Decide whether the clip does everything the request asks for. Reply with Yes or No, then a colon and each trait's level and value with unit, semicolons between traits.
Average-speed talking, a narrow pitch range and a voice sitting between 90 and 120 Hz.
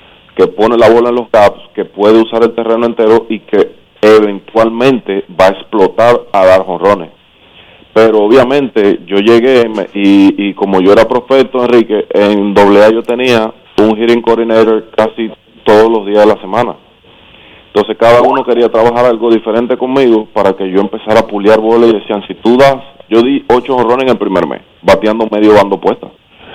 Yes: average, 180 wpm; narrow, 2.1 semitones; low, 110 Hz